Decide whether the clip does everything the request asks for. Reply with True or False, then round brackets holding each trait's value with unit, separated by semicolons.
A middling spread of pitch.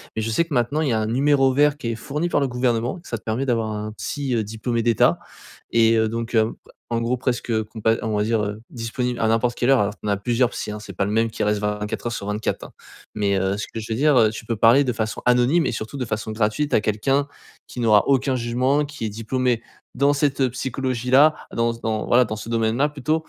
True (3.2 semitones)